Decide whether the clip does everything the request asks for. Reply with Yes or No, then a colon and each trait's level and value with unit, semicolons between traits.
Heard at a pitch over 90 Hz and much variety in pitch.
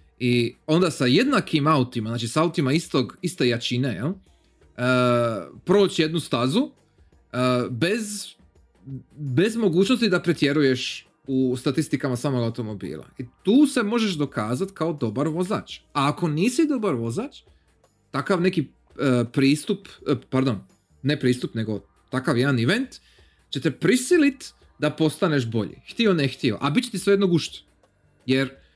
Yes: low, 135 Hz; wide, 6.6 semitones